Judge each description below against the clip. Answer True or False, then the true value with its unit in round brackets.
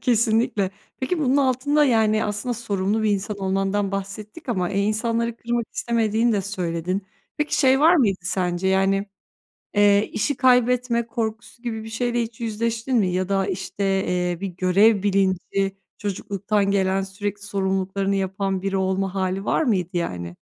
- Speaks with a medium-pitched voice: False (205 Hz)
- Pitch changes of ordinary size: True (3.3 semitones)